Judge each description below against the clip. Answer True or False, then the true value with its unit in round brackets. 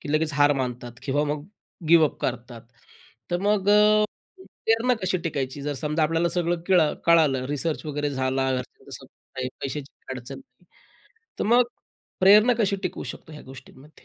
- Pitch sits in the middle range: True (150 Hz)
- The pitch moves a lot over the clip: True (5.7 semitones)